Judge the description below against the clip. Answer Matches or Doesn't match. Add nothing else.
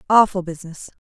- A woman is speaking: Matches